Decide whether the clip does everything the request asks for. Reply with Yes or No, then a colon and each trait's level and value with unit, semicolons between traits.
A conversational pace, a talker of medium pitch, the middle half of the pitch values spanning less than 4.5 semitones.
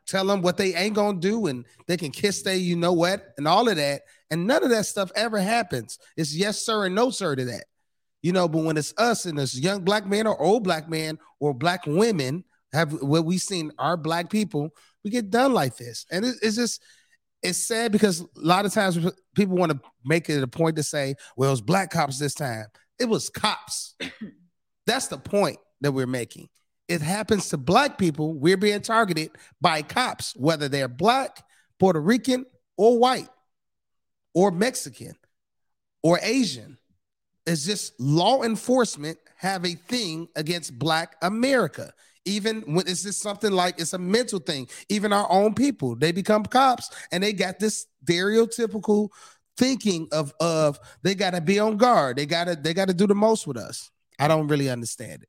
No: average, 190 wpm; medium, 180 Hz; average, 5.2 semitones